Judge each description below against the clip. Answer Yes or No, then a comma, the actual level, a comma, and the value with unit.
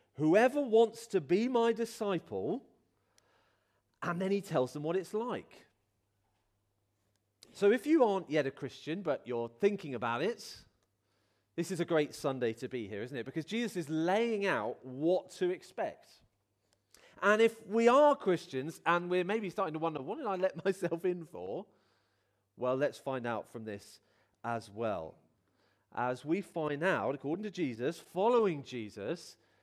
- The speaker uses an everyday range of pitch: No, wide, 8.8 semitones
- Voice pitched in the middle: Yes, medium, 160 Hz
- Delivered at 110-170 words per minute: Yes, average, 160 wpm